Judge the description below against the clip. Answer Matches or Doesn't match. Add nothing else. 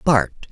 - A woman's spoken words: Doesn't match